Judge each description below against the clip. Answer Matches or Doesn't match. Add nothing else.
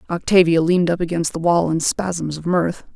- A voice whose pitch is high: Doesn't match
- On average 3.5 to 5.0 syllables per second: Doesn't match